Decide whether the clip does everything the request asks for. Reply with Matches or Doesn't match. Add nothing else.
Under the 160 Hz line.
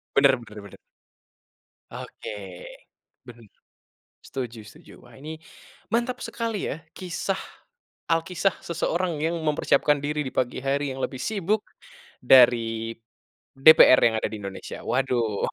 Matches